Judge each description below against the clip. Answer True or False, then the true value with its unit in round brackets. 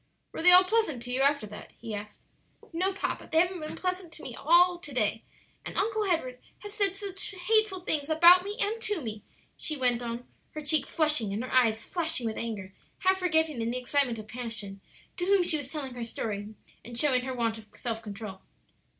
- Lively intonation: True (7.7 semitones)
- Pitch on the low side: False (285 Hz)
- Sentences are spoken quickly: True (210 wpm)